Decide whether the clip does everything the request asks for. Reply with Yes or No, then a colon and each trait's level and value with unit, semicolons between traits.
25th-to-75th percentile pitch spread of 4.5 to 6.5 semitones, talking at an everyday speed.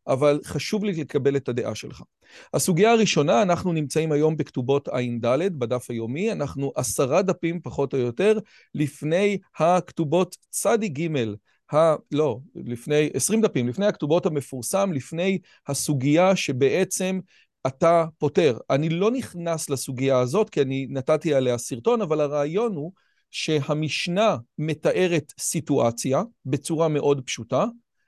Yes: wide, 5.5 semitones; average, 125 wpm